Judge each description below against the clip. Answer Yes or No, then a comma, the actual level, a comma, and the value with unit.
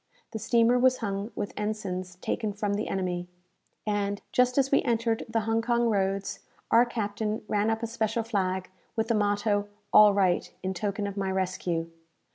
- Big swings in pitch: No, narrow, 2.5 semitones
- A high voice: Yes, high, 210 Hz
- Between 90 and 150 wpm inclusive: No, average, 175 wpm